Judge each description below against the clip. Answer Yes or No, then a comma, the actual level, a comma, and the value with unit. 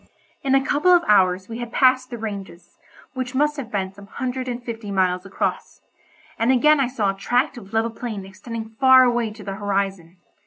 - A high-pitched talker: Yes, high, 230 Hz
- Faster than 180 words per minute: Yes, average, 200 wpm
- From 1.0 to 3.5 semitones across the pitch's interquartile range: No, average, 4.6 semitones